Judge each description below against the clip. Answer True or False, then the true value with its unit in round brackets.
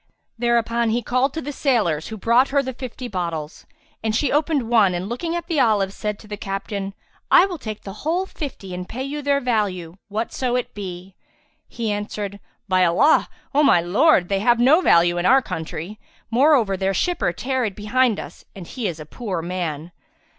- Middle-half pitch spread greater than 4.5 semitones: True (5.6 semitones)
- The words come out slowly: False (195 wpm)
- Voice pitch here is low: False (220 Hz)